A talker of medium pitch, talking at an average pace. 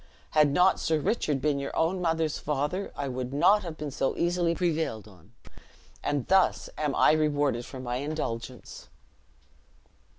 Yes: medium, 150 Hz; average, 155 wpm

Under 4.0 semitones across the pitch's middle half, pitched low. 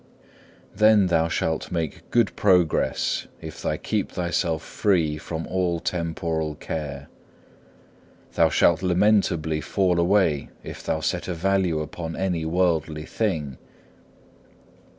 Yes: average, 2.7 semitones; very low, 85 Hz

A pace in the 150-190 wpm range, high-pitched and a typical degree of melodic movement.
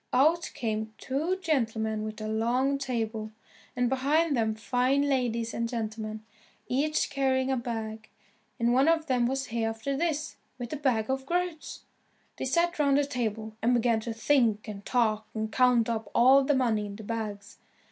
Yes: average, 165 wpm; high, 240 Hz; average, 3.7 semitones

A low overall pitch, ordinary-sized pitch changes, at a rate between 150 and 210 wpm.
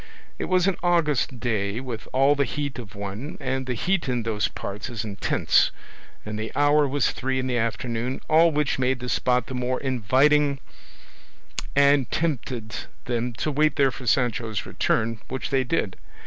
Yes: low, 130 Hz; average, 3.8 semitones; average, 175 wpm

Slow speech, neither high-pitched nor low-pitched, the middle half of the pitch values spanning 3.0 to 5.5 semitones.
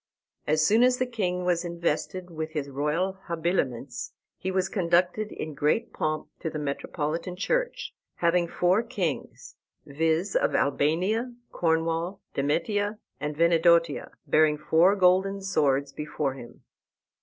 Yes: slow, 130 wpm; medium, 170 Hz; average, 3.8 semitones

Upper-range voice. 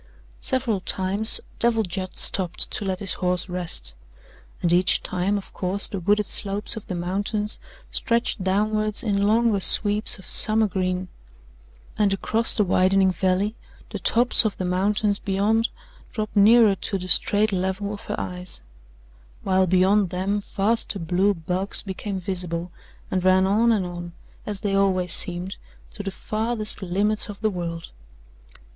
Yes: high, 195 Hz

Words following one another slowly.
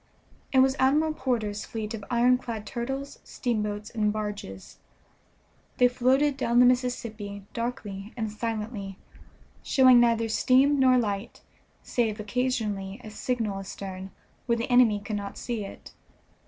Yes: slow, 130 wpm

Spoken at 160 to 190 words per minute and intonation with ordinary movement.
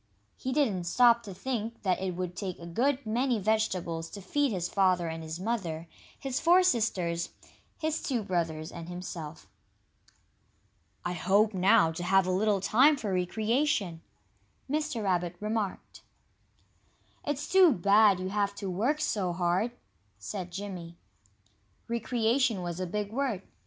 No: average, 145 wpm; average, 4.9 semitones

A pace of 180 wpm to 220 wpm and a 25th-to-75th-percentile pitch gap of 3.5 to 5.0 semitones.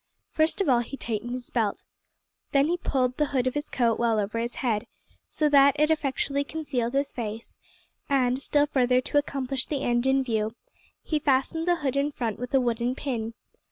No: average, 195 wpm; average, 3.1 semitones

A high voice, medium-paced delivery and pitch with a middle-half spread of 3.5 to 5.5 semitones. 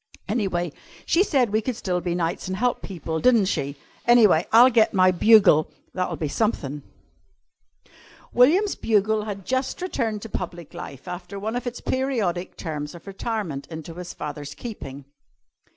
Yes: high, 195 Hz; average, 155 wpm; average, 5.2 semitones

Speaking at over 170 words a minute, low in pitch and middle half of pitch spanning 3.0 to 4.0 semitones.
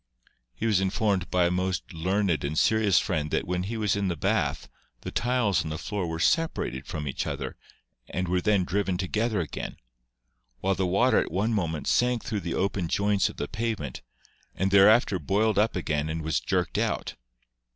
Yes: average, 195 wpm; very low, 95 Hz; average, 3.7 semitones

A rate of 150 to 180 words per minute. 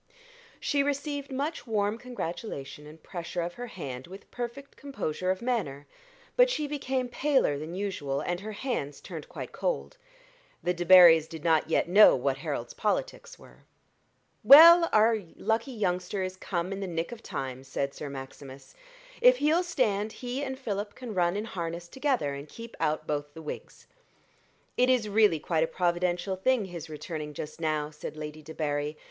Yes: average, 170 wpm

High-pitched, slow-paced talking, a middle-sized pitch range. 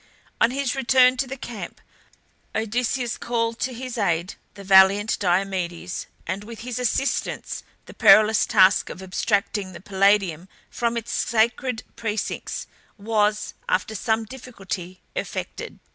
Yes: high, 215 Hz; slow, 130 wpm; average, 3.8 semitones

